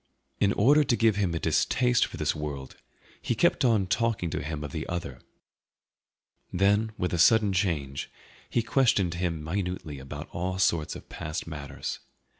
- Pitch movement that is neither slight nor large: No, wide, 5.7 semitones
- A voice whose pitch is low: Yes, very low, 90 Hz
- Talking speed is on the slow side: No, average, 165 wpm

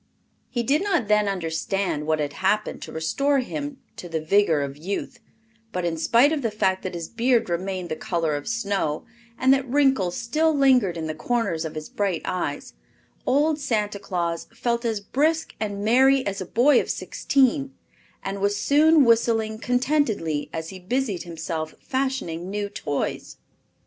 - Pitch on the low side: No, high, 205 Hz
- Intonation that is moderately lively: No, wide, 7.2 semitones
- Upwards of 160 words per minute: Yes, average, 170 wpm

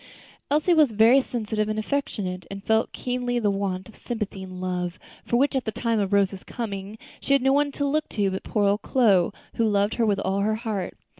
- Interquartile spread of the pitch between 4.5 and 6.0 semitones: No, average, 3.7 semitones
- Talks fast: Yes, fast, 220 wpm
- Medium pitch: No, high, 215 Hz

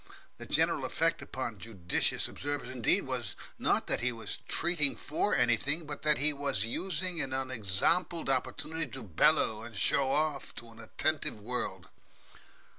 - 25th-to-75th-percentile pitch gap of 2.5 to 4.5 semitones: No, average, 5.0 semitones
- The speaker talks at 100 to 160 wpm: Yes, average, 150 wpm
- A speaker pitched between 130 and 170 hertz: Yes, low, 135 Hz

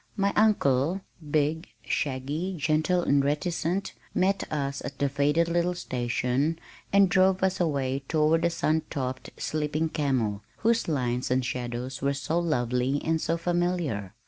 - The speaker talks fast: No, average, 145 wpm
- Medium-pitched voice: Yes, medium, 150 Hz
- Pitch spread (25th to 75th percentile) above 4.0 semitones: Yes, average, 4.6 semitones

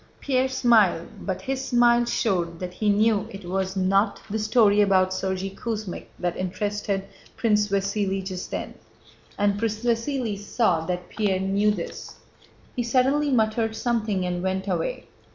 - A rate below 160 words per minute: Yes, average, 150 wpm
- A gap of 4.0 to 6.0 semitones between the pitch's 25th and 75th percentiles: No, average, 3.3 semitones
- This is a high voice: Yes, high, 205 Hz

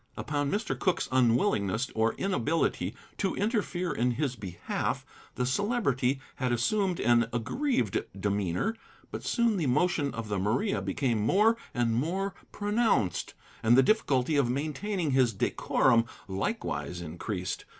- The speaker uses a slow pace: Yes, slow, 130 wpm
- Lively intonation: Yes, wide, 9.0 semitones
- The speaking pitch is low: Yes, low, 130 Hz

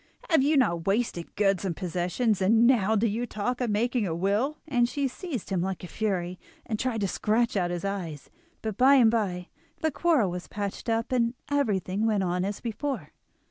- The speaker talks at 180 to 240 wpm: Yes, average, 200 wpm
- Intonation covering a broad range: No, average, 4.5 semitones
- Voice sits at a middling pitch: No, high, 215 Hz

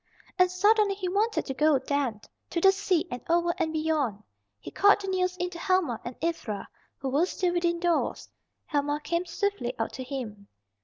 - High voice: Yes, very high, 340 Hz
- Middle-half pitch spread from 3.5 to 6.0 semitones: Yes, average, 5.1 semitones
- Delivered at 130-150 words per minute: No, average, 190 wpm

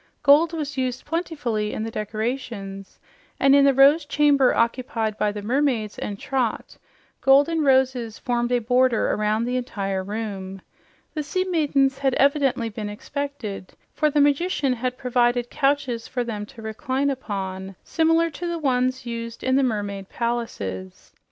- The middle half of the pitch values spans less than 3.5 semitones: No, average, 4.5 semitones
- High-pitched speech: Yes, very high, 250 Hz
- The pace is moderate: Yes, average, 150 wpm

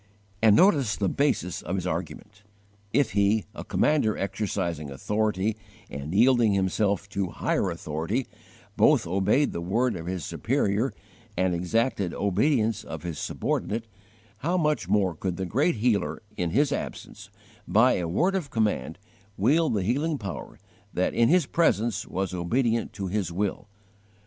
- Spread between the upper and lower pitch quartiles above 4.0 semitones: Yes, average, 4.9 semitones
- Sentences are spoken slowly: No, average, 150 wpm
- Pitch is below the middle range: Yes, low, 105 Hz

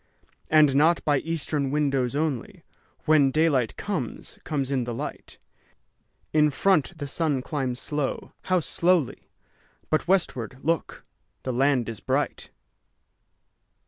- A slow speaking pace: Yes, slow, 110 wpm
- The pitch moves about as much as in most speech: Yes, average, 3.2 semitones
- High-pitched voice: No, medium, 145 Hz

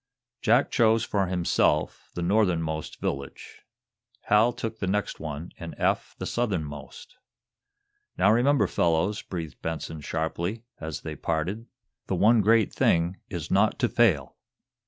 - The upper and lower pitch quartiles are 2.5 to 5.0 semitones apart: No, wide, 5.4 semitones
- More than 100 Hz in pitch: No, very low, 95 Hz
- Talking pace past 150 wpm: No, slow, 135 wpm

